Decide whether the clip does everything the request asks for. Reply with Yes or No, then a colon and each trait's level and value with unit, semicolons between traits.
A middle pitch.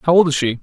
Yes: medium, 150 Hz